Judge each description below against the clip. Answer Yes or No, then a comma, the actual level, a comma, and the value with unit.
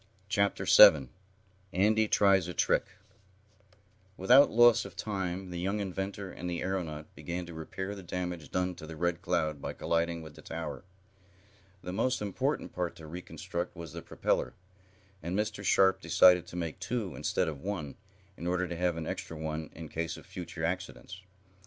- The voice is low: Yes, very low, 90 Hz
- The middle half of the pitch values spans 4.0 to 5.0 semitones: No, average, 2.7 semitones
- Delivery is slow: No, average, 170 wpm